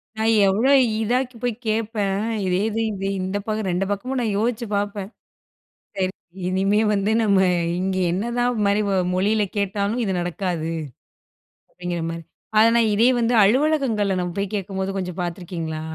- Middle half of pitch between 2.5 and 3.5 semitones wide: Yes, average, 2.9 semitones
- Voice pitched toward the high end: Yes, high, 200 Hz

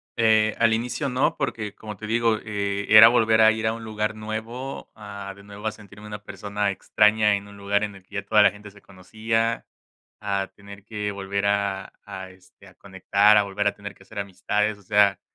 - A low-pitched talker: Yes, low, 105 Hz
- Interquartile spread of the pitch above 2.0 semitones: No, narrow, 1.5 semitones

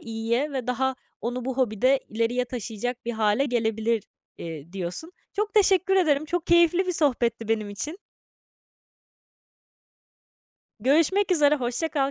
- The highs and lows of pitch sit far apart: Yes, wide, 5.7 semitones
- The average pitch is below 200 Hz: No, very high, 250 Hz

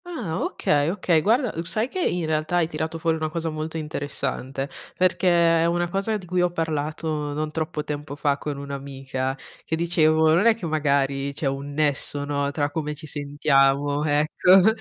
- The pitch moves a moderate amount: Yes, average, 3.0 semitones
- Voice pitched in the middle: Yes, medium, 155 Hz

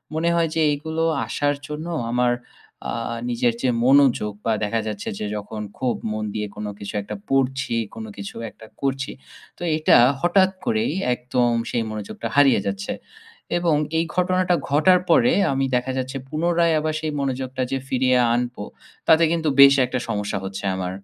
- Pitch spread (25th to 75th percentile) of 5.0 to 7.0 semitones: Yes, wide, 5.5 semitones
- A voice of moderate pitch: No, low, 130 Hz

